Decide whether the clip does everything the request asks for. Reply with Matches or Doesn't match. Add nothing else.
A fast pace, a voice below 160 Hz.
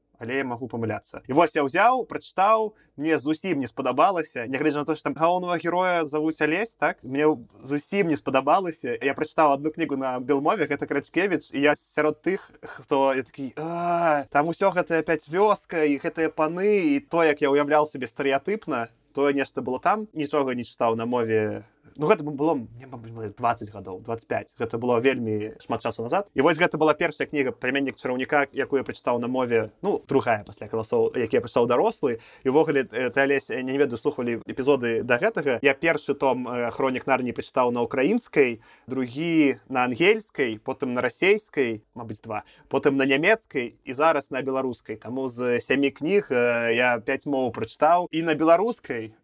Matches